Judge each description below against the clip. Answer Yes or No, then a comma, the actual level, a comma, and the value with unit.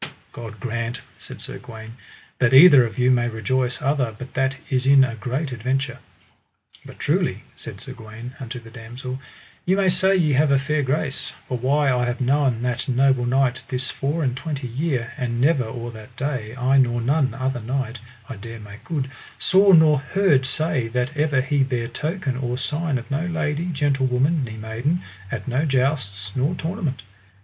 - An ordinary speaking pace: Yes, average, 185 wpm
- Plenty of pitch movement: No, average, 3.2 semitones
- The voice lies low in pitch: Yes, low, 130 Hz